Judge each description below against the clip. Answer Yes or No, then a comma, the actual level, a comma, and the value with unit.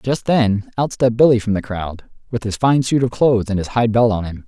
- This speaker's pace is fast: Yes, fast, 270 wpm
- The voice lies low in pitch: Yes, low, 115 Hz